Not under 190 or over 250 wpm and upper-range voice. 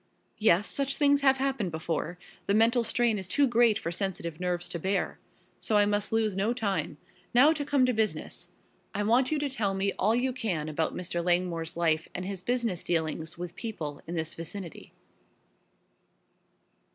No: average, 175 wpm; high, 200 Hz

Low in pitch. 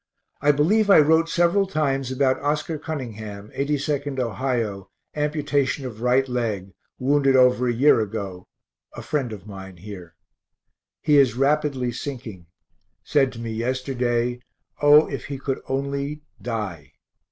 Yes: low, 130 Hz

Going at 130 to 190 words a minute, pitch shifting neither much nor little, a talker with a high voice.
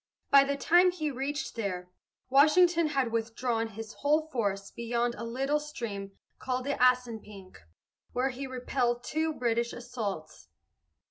Yes: slow, 135 wpm; average, 3.7 semitones; very high, 250 Hz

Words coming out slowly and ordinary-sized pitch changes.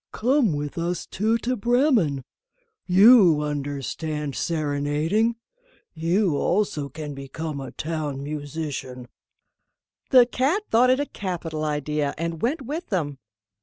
No: slow, 120 wpm; wide, 7.3 semitones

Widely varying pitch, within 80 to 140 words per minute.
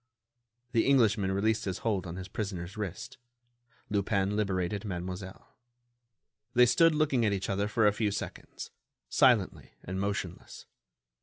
No: narrow, 2.6 semitones; slow, 135 wpm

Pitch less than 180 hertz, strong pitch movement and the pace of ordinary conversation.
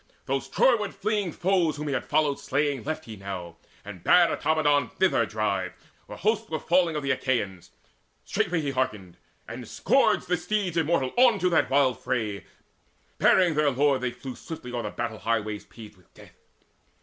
Yes: medium, 140 Hz; wide, 6.9 semitones; average, 175 wpm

